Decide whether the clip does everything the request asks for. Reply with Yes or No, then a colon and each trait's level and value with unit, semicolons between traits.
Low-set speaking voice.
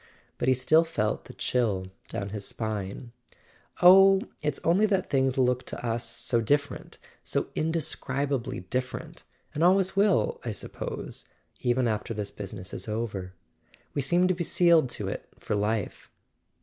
Yes: low, 130 Hz